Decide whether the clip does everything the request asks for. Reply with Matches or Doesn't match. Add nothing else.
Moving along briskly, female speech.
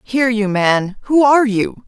Doesn't match